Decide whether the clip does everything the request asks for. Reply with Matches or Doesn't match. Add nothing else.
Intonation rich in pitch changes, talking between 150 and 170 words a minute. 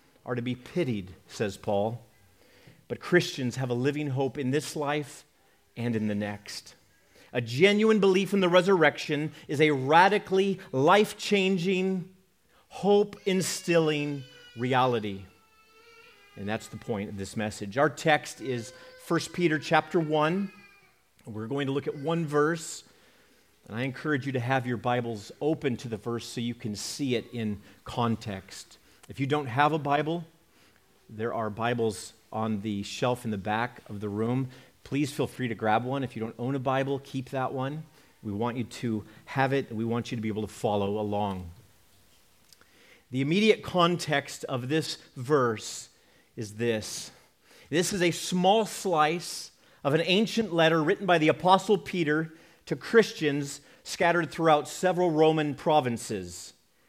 Matches